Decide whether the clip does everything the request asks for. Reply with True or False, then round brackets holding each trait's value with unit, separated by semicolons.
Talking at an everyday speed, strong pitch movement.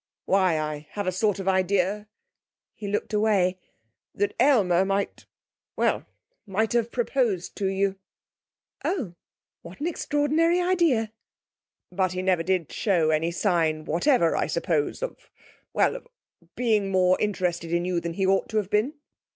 False (150 wpm; 3.8 semitones)